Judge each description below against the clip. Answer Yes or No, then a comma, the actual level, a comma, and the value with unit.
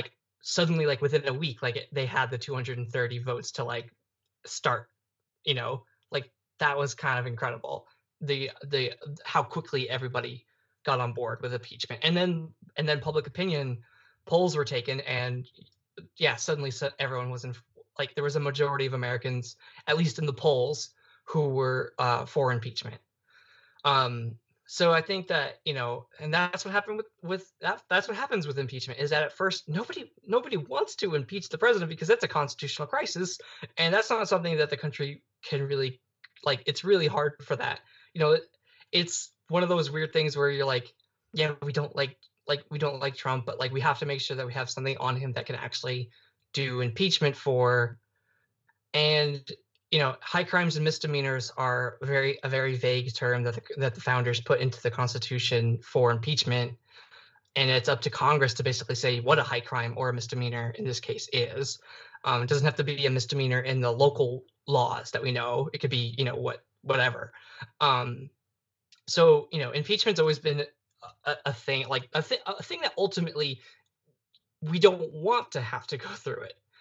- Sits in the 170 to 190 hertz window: No, medium, 140 Hz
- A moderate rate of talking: Yes, average, 190 wpm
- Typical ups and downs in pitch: Yes, average, 3.6 semitones